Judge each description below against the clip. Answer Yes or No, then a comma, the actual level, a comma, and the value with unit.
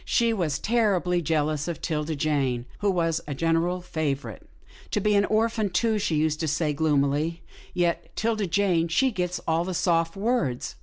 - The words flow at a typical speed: Yes, average, 175 wpm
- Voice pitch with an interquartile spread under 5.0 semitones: Yes, average, 4.6 semitones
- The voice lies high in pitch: No, medium, 170 Hz